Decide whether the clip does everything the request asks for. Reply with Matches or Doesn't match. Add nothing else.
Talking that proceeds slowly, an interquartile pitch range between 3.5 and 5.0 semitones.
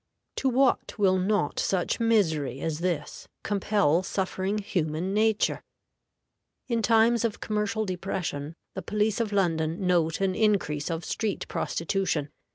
Matches